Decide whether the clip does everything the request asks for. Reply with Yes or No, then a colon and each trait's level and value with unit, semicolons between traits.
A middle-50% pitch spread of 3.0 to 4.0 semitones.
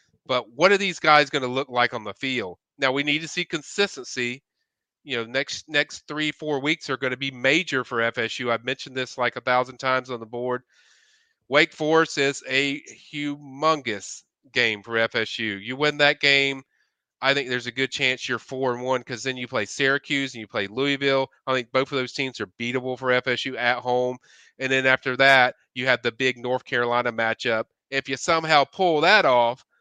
No: narrow, 2.5 semitones